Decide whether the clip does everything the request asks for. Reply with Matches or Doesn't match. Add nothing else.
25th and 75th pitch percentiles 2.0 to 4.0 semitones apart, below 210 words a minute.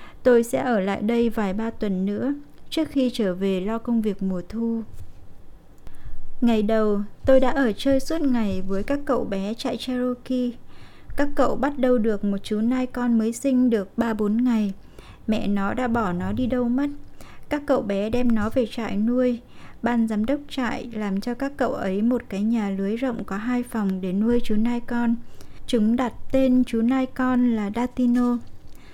Matches